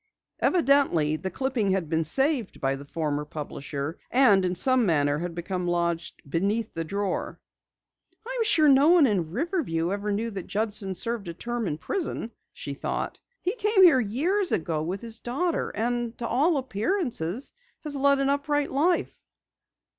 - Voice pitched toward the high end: Yes, high, 220 Hz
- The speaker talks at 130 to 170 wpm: Yes, average, 160 wpm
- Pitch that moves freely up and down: Yes, wide, 8.5 semitones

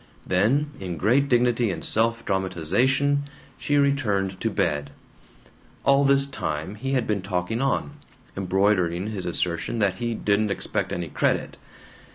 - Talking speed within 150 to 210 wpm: No, average, 140 wpm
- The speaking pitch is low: Yes, low, 105 Hz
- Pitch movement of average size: No, wide, 6.3 semitones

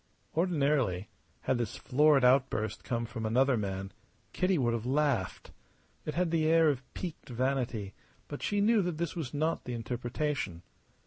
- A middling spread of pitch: Yes, average, 5.0 semitones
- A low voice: Yes, low, 130 Hz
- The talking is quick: No, average, 155 wpm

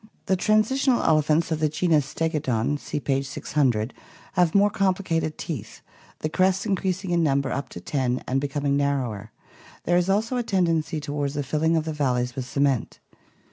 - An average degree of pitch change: Yes, average, 4.6 semitones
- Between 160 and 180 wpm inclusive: Yes, average, 170 wpm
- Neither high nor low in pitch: Yes, medium, 155 Hz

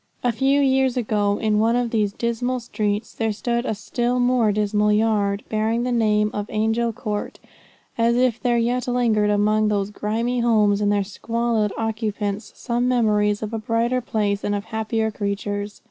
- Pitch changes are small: Yes, narrow, 2.3 semitones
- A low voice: No, high, 220 Hz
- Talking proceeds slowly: No, average, 175 wpm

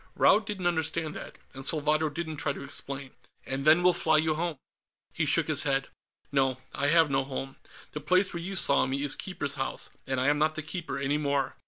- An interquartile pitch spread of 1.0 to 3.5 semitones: Yes, average, 2.9 semitones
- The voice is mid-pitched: Yes, medium, 150 Hz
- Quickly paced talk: Yes, fast, 215 wpm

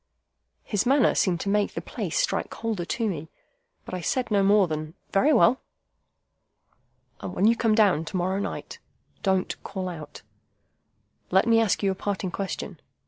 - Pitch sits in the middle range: No, high, 200 Hz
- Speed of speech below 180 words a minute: Yes, average, 170 wpm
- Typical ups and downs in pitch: Yes, average, 3.4 semitones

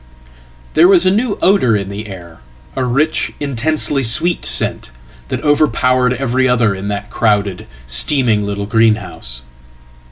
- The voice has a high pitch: No, low, 120 Hz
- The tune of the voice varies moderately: No, wide, 6.4 semitones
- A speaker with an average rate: No, slow, 130 wpm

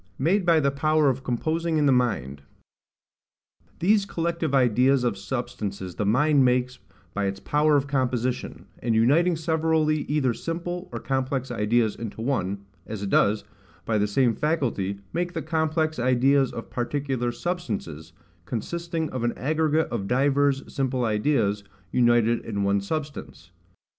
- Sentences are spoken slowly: No, average, 145 wpm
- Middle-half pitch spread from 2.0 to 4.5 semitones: No, average, 5.3 semitones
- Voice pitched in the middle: No, low, 130 Hz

